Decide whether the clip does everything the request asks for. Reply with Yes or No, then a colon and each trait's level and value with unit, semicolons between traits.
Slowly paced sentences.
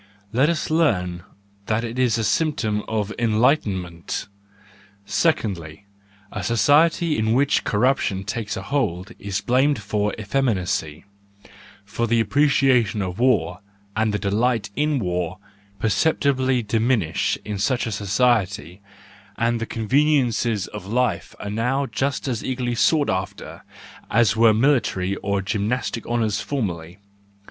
Yes: slow, 125 wpm